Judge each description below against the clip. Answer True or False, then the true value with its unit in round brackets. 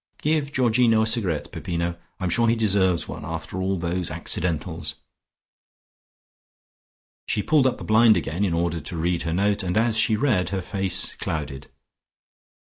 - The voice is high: False (95 Hz)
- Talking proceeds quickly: False (160 wpm)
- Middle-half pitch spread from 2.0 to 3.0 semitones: False (4.7 semitones)